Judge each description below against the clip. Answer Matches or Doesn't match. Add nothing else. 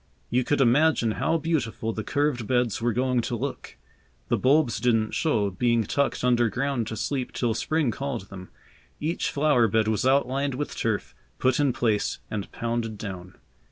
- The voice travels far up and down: Doesn't match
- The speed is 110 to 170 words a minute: Matches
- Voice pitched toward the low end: Matches